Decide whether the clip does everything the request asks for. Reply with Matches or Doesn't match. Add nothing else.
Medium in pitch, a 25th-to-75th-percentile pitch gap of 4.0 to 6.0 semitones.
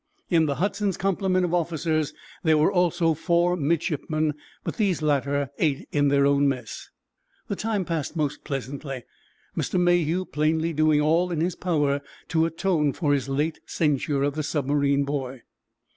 Doesn't match